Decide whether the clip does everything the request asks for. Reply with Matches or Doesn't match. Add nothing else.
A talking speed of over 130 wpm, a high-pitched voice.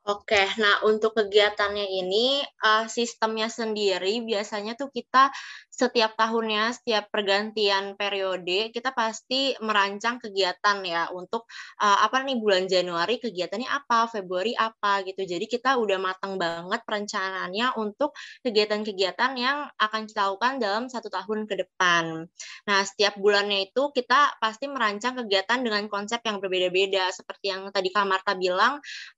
Matches